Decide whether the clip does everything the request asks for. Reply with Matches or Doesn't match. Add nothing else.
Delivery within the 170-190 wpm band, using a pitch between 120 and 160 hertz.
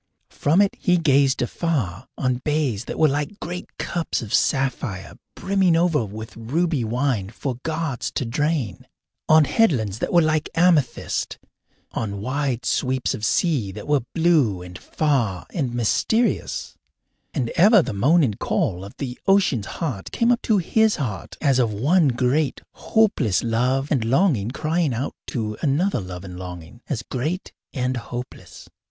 Doesn't match